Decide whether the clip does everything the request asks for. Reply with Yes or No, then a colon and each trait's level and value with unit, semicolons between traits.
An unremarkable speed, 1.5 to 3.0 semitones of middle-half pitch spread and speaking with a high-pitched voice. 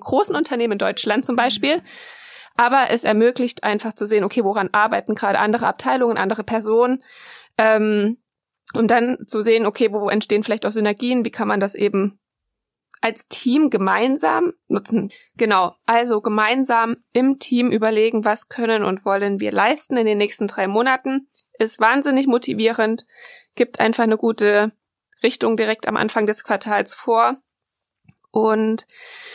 Yes: average, 150 wpm; narrow, 2.5 semitones; high, 225 Hz